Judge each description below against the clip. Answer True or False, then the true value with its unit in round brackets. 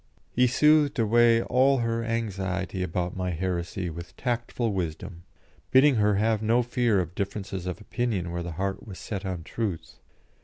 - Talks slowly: False (160 wpm)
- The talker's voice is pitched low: True (105 Hz)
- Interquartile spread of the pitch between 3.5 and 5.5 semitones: True (4.4 semitones)